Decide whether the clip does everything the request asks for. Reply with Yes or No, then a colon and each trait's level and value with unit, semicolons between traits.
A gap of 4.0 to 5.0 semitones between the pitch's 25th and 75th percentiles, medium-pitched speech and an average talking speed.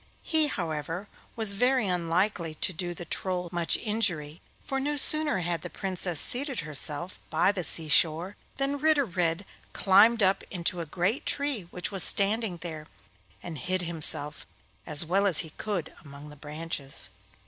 Yes: average, 4.5 semitones; medium, 180 Hz; average, 160 wpm